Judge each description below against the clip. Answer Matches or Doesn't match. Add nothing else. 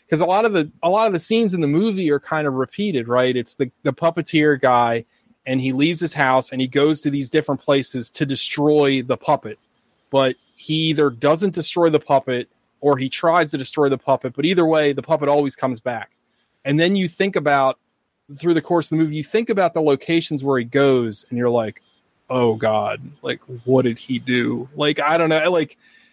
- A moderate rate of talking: Doesn't match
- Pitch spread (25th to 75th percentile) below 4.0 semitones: Matches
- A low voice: Doesn't match